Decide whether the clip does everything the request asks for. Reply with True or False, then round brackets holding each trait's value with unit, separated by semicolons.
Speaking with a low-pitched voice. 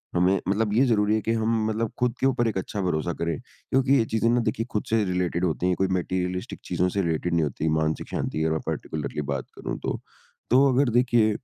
True (100 Hz)